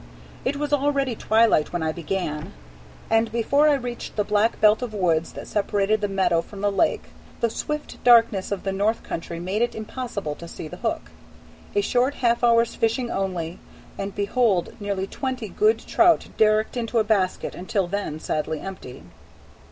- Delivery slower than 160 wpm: No, average, 175 wpm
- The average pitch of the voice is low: No, high, 215 Hz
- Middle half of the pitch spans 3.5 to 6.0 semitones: Yes, average, 4.1 semitones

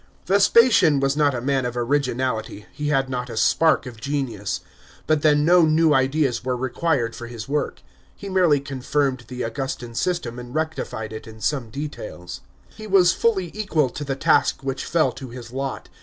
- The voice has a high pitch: No, low, 135 Hz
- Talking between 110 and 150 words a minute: No, average, 180 wpm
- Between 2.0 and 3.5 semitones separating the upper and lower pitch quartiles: No, average, 4.2 semitones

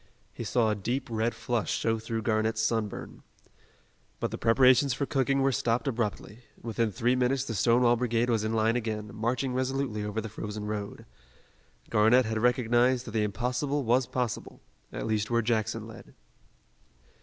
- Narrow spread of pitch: Yes, narrow, 2.3 semitones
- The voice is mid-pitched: No, low, 115 Hz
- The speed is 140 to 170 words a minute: Yes, average, 165 wpm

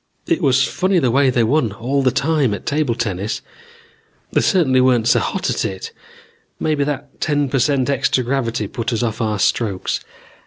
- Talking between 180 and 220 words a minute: Yes, average, 185 wpm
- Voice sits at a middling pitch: No, low, 130 Hz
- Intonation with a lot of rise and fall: No, average, 3.5 semitones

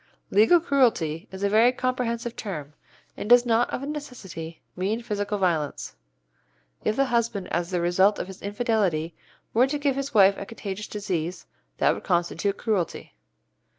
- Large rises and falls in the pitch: No, average, 4.9 semitones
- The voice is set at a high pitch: Yes, high, 205 Hz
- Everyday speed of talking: Yes, average, 155 wpm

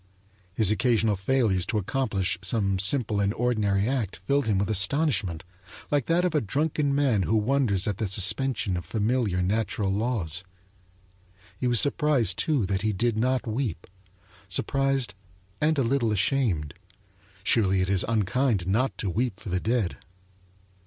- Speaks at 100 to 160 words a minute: Yes, average, 150 wpm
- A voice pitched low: Yes, low, 110 Hz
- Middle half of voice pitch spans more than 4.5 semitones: Yes, average, 5.1 semitones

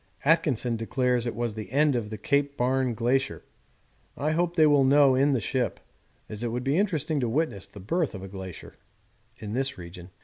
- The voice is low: Yes, low, 130 Hz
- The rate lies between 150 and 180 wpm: No, average, 200 wpm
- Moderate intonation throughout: Yes, average, 4.5 semitones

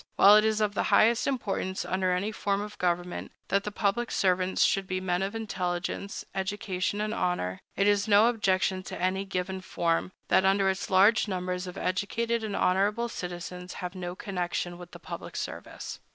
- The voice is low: No, high, 190 Hz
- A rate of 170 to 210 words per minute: Yes, average, 180 wpm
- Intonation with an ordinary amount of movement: No, narrow, 2.2 semitones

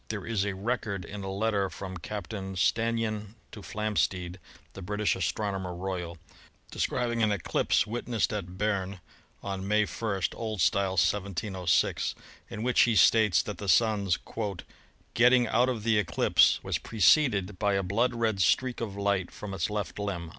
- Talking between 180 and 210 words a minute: No, average, 160 wpm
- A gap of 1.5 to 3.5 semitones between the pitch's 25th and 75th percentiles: Yes, narrow, 2.6 semitones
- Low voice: Yes, low, 100 Hz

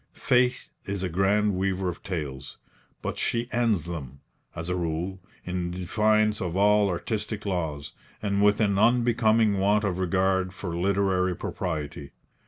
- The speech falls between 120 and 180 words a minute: Yes, average, 145 wpm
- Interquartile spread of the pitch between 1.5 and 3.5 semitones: Yes, average, 3.0 semitones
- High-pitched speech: No, very low, 95 Hz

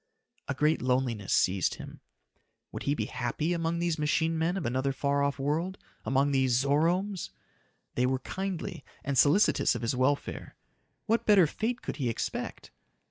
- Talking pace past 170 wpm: No, average, 160 wpm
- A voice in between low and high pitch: Yes, medium, 145 Hz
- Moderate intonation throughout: Yes, average, 4.5 semitones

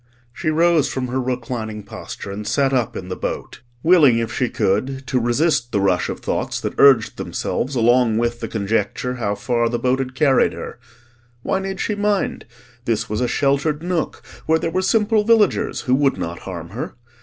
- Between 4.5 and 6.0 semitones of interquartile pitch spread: Yes, average, 5.3 semitones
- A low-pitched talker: Yes, low, 125 Hz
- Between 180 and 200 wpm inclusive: Yes, average, 190 wpm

